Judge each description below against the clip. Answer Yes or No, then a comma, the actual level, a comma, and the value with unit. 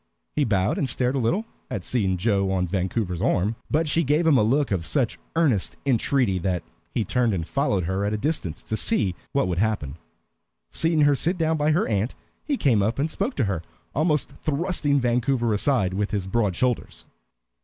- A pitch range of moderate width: No, wide, 7.0 semitones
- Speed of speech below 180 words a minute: No, average, 195 wpm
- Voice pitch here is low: Yes, low, 115 Hz